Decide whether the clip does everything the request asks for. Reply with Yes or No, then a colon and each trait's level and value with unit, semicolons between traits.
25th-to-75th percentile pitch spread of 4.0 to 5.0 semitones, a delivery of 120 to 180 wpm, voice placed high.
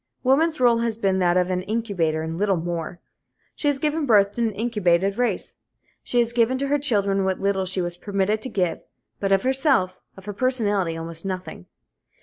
No: average, 4.7 semitones; average, 195 wpm; high, 200 Hz